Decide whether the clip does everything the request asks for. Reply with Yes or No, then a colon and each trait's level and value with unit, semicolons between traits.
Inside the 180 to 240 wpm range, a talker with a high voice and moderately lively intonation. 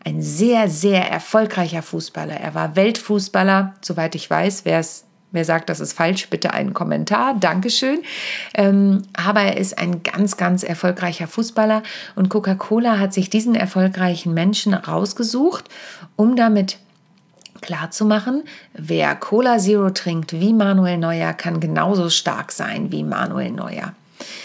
No: average, 130 wpm; high, 195 Hz; average, 3.6 semitones